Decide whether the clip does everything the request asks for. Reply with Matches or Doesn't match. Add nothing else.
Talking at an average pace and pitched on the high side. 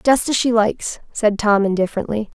Matches